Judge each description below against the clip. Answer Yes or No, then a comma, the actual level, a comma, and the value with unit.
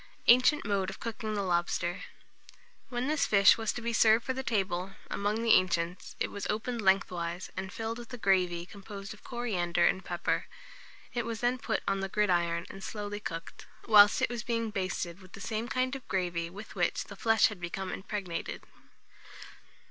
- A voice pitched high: Yes, high, 200 Hz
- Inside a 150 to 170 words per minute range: No, average, 185 wpm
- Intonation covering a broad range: No, average, 3.8 semitones